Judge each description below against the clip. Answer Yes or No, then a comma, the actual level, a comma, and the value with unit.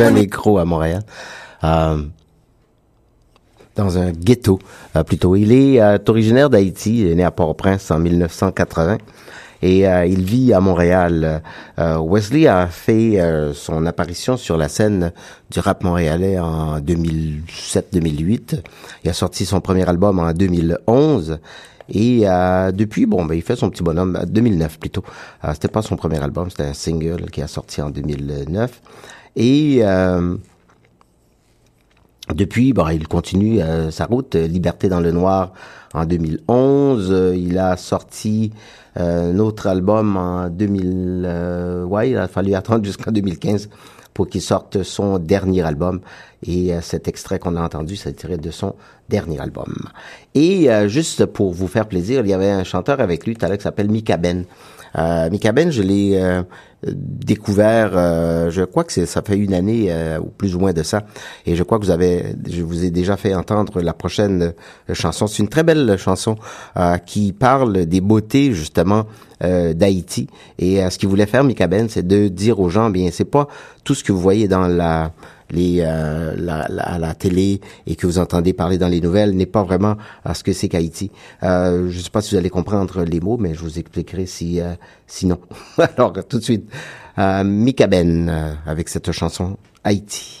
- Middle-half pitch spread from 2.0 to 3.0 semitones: No, average, 3.5 semitones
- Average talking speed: Yes, average, 180 wpm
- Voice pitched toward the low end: Yes, very low, 95 Hz